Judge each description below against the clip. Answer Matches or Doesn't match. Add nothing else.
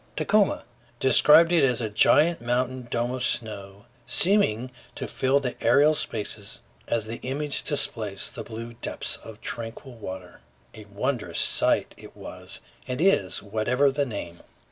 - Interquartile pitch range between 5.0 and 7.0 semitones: Doesn't match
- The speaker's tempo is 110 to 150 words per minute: Matches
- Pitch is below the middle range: Matches